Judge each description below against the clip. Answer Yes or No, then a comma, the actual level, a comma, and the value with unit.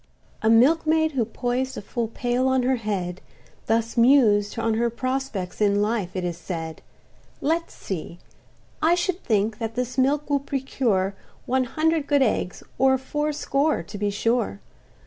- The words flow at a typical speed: Yes, average, 150 wpm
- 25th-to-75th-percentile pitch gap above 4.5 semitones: Yes, average, 4.9 semitones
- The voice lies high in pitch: Yes, high, 240 Hz